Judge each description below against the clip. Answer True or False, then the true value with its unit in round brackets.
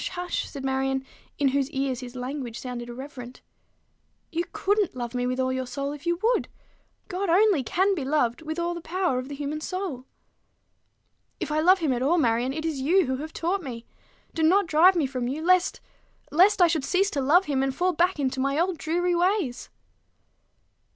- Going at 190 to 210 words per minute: True (200 wpm)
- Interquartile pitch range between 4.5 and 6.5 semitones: True (5.2 semitones)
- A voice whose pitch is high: True (300 Hz)